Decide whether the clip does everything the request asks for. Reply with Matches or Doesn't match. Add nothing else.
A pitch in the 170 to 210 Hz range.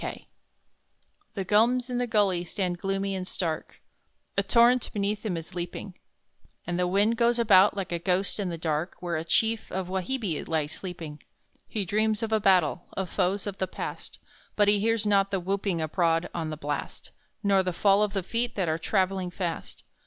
Matches